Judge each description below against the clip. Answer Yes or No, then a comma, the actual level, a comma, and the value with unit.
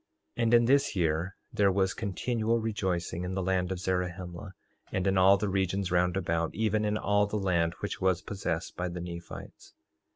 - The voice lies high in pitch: No, very low, 95 Hz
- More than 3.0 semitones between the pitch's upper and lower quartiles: No, narrow, 2.5 semitones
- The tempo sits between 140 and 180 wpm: No, average, 190 wpm